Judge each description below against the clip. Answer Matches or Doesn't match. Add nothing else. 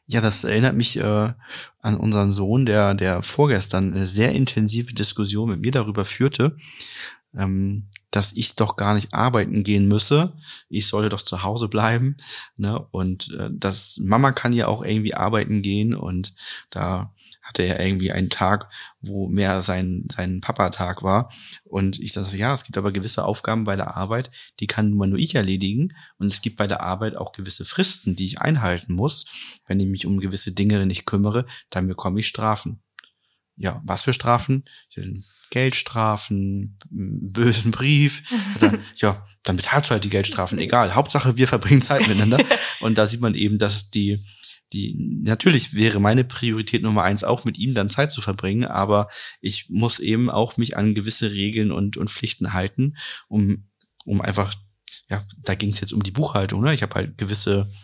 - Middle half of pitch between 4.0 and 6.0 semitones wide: Doesn't match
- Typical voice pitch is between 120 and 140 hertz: Doesn't match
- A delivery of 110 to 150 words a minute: Doesn't match